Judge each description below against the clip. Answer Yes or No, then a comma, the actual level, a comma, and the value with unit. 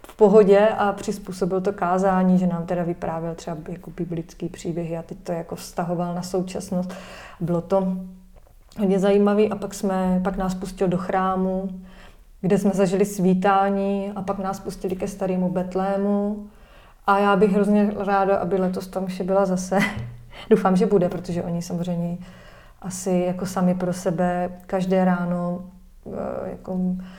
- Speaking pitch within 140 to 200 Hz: Yes, high, 190 Hz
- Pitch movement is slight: Yes, narrow, 1.6 semitones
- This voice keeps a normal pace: Yes, average, 150 wpm